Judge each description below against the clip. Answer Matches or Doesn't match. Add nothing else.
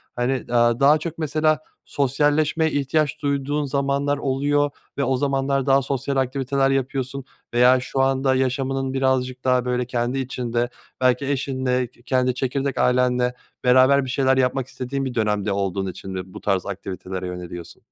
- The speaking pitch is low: Matches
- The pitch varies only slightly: Matches